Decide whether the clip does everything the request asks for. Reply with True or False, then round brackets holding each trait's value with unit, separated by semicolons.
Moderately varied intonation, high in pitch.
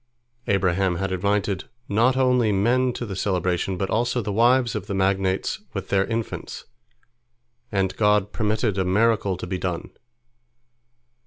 False (3.3 semitones; 100 Hz)